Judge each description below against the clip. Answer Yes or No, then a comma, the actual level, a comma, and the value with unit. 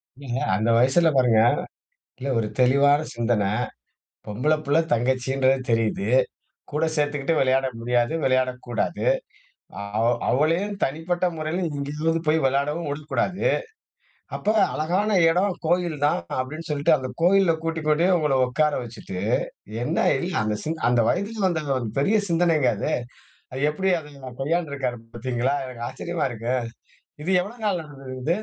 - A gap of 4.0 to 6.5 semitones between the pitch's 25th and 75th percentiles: Yes, average, 4.5 semitones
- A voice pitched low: No, medium, 145 Hz